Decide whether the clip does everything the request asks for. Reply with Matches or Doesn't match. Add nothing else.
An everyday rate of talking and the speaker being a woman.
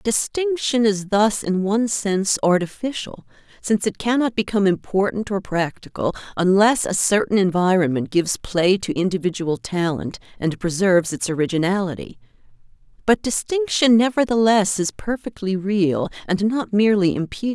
Doesn't match